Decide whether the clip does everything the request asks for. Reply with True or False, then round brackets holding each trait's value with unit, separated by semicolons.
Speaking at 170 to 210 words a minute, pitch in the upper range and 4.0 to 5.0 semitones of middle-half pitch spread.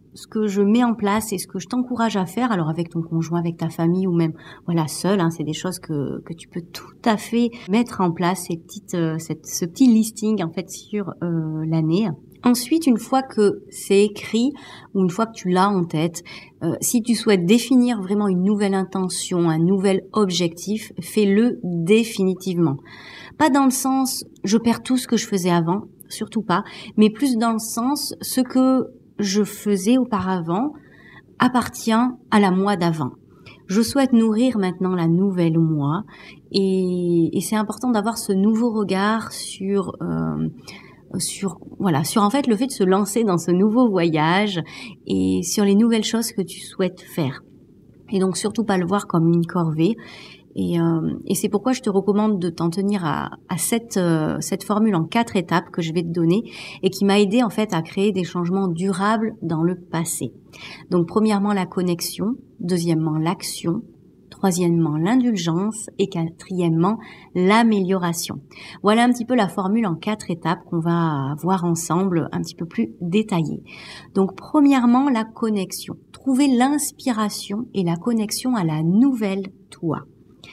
True (175 wpm; 195 Hz; 4.3 semitones)